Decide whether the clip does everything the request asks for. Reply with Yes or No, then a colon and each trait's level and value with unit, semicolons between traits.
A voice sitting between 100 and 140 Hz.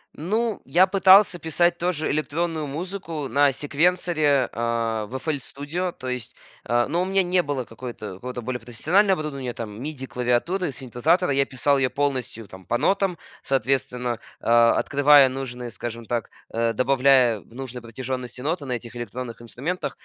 Yes: low, 135 Hz